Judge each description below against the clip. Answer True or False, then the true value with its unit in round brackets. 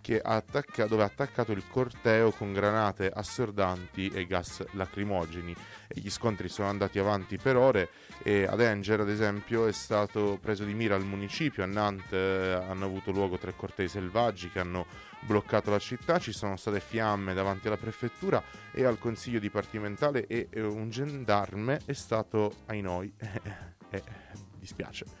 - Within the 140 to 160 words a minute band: True (155 wpm)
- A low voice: True (105 Hz)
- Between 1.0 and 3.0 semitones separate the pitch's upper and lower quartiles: True (2.4 semitones)